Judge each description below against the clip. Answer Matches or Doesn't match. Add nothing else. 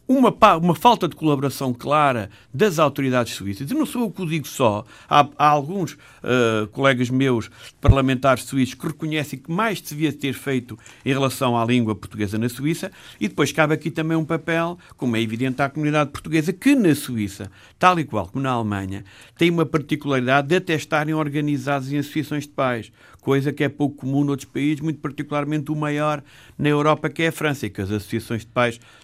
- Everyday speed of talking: Doesn't match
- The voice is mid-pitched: Matches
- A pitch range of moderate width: Matches